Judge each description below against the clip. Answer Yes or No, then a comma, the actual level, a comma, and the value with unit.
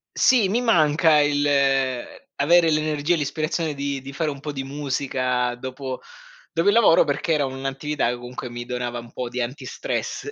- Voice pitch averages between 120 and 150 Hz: Yes, medium, 140 Hz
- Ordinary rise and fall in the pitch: Yes, average, 3.1 semitones